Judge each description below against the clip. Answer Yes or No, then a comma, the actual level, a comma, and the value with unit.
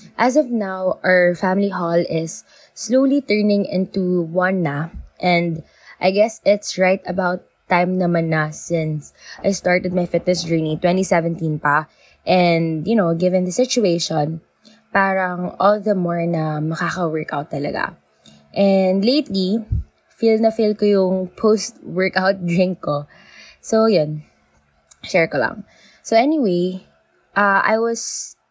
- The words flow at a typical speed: Yes, average, 130 wpm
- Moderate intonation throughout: Yes, average, 3.4 semitones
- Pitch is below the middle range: No, medium, 185 Hz